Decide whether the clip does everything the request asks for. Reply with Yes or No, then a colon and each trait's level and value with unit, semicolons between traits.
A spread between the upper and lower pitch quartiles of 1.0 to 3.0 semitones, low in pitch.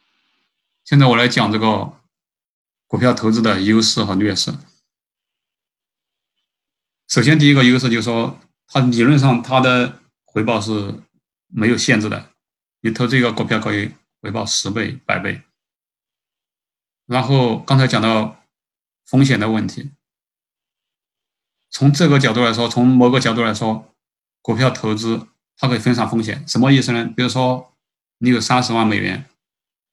Yes: narrow, 2.4 semitones; low, 120 Hz